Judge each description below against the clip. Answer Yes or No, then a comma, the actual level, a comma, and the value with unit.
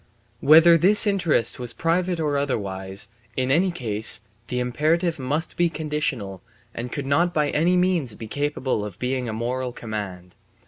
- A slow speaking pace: No, average, 155 wpm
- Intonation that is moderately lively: No, wide, 6.3 semitones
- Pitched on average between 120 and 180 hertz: Yes, medium, 140 Hz